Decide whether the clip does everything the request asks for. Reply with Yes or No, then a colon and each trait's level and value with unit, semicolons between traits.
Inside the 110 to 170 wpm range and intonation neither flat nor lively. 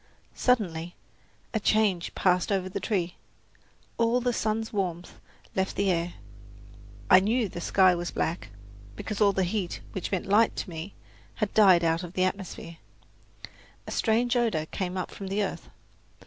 Yes: average, 160 wpm; average, 3.4 semitones